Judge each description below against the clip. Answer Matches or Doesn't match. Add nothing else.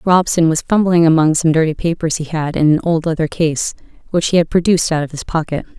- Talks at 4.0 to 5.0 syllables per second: Doesn't match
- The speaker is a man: Doesn't match